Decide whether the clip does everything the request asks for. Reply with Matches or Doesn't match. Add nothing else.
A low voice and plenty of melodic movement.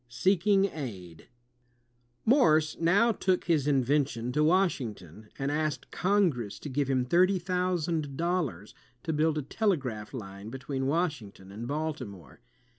Doesn't match